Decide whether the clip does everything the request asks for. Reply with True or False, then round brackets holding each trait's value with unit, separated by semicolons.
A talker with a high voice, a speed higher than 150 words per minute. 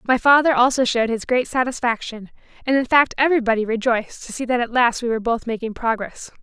True (240 Hz; 205 wpm)